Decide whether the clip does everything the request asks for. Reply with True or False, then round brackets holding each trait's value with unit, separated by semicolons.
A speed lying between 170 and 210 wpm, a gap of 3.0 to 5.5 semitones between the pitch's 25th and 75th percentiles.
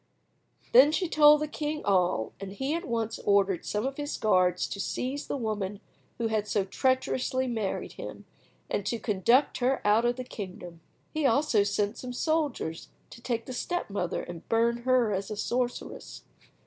True (175 wpm; 4.5 semitones)